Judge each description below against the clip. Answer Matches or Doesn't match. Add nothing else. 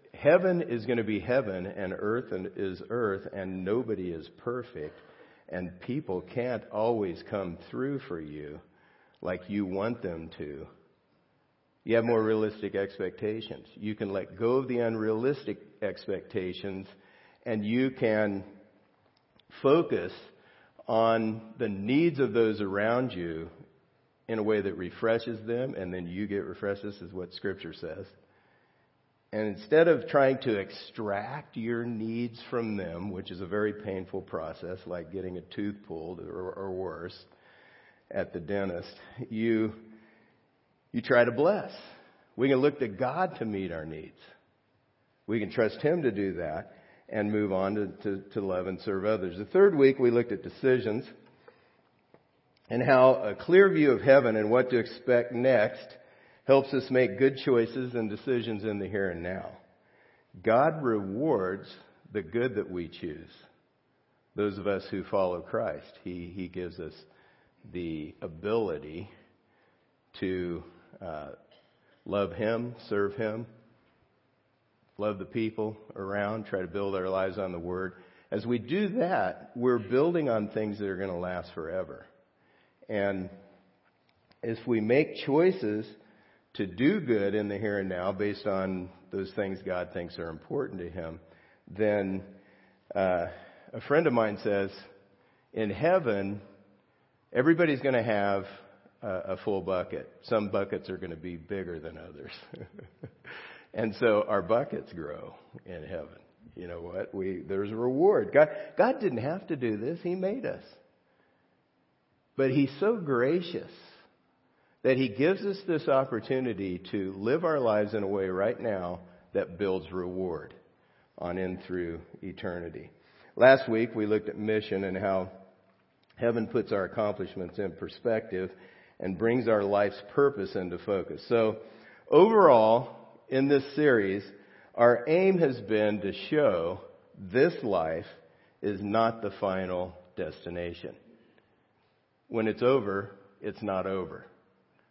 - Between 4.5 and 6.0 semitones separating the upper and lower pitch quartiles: Doesn't match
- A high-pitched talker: Doesn't match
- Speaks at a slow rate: Doesn't match